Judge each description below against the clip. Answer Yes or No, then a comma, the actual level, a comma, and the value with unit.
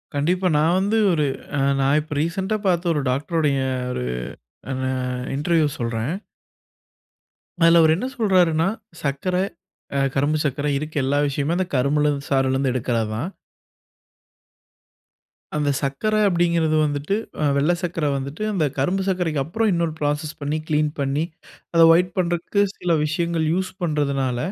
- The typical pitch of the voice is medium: Yes, medium, 155 Hz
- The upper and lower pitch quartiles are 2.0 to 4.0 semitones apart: Yes, average, 3.7 semitones